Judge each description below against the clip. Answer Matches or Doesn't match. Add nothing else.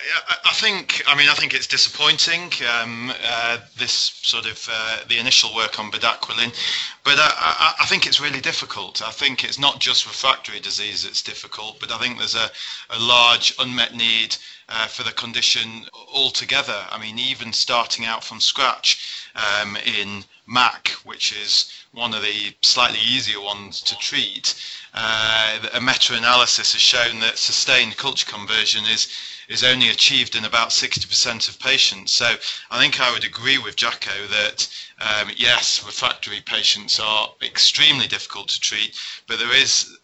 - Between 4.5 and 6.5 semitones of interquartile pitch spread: Doesn't match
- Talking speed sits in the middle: Matches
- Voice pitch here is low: Matches